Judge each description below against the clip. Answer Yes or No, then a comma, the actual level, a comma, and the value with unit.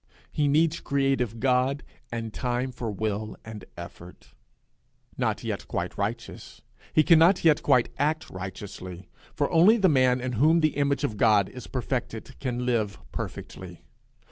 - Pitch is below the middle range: Yes, low, 125 Hz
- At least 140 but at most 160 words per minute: Yes, average, 145 wpm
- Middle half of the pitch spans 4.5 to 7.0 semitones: Yes, average, 4.8 semitones